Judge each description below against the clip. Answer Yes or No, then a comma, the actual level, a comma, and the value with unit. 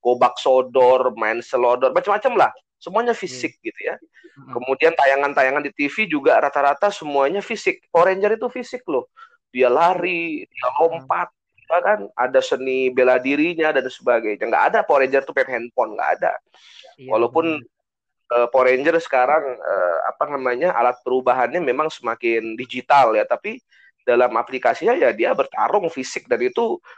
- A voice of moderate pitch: Yes, medium, 145 Hz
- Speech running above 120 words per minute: Yes, fast, 140 wpm